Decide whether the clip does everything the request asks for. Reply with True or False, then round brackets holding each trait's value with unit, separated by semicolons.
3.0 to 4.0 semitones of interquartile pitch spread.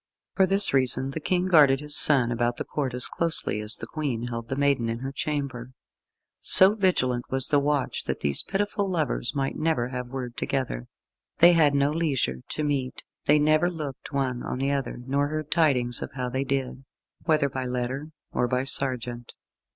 True (3.4 semitones)